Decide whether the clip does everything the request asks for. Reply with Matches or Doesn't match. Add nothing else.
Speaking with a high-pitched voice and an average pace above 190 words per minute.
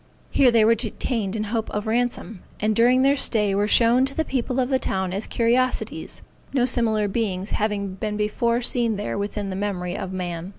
Matches